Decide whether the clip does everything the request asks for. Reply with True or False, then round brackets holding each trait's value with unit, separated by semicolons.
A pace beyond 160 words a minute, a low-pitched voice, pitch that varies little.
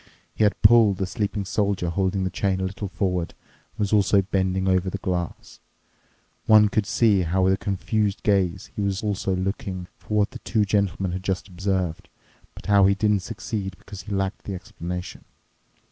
True (185 wpm; 95 Hz; 1.7 semitones)